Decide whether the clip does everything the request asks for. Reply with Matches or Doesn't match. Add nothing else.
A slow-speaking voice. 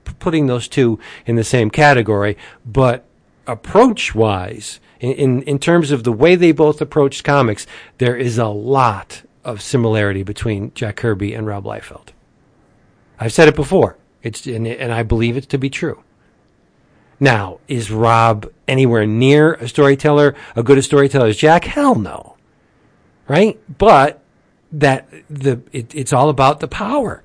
Doesn't match